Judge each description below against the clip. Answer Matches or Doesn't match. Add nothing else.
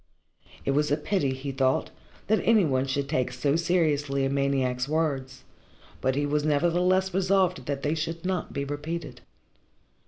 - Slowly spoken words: Doesn't match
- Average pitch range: Matches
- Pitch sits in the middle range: Matches